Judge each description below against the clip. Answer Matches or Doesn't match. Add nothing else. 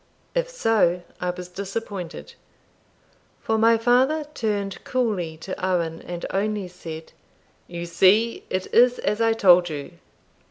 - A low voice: Doesn't match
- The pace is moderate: Doesn't match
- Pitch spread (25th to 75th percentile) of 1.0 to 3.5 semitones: Doesn't match